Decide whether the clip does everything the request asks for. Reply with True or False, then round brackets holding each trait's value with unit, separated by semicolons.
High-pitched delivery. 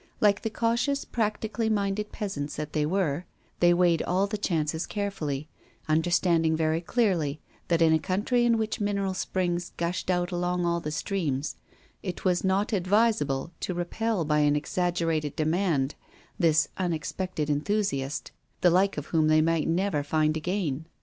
False (175 Hz)